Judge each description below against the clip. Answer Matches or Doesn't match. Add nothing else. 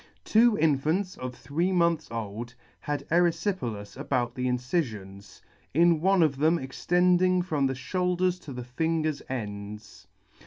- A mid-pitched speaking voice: Matches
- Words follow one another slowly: Matches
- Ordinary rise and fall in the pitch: Doesn't match